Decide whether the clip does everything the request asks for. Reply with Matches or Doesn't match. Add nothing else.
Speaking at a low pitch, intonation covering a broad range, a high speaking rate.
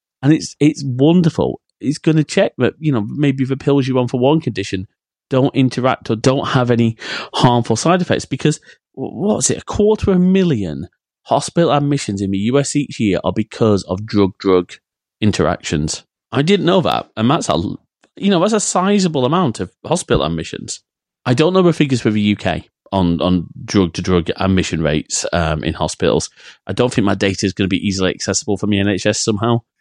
Doesn't match